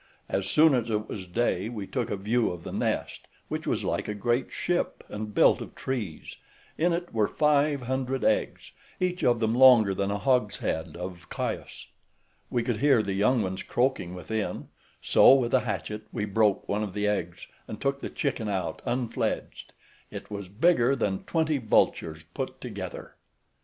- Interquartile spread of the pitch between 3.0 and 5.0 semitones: Yes, average, 4.6 semitones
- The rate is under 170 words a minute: No, average, 180 wpm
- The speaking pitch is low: Yes, low, 110 Hz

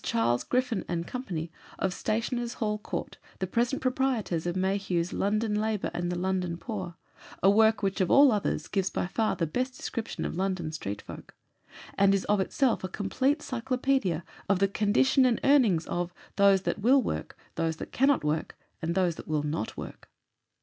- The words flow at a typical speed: Yes, average, 180 wpm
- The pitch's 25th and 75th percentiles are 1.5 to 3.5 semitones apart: No, average, 5.2 semitones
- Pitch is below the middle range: No, high, 195 Hz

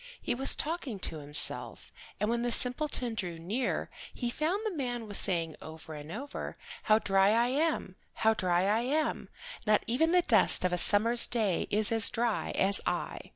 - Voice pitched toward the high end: Yes, high, 225 Hz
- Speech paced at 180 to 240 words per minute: Yes, average, 185 wpm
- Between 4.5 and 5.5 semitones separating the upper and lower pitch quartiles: Yes, average, 4.8 semitones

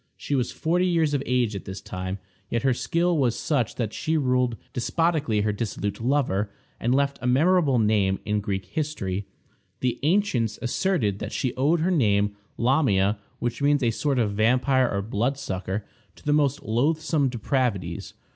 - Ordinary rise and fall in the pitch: No, wide, 5.7 semitones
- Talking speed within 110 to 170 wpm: Yes, average, 165 wpm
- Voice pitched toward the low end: Yes, low, 125 Hz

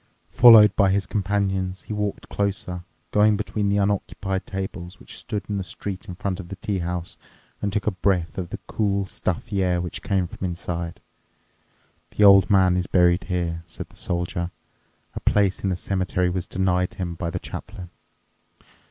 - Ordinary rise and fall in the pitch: No, narrow, 2.2 semitones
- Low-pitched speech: Yes, very low, 95 Hz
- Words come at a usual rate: Yes, average, 180 wpm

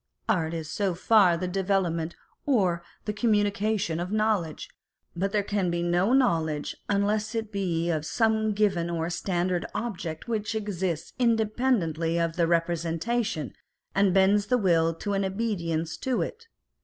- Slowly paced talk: No, average, 150 wpm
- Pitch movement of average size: Yes, average, 4.2 semitones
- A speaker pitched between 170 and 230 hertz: Yes, high, 190 Hz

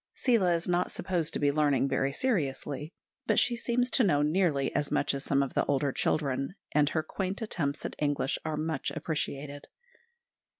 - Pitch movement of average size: Yes, average, 4.1 semitones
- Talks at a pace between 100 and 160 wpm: No, average, 180 wpm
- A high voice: No, medium, 150 Hz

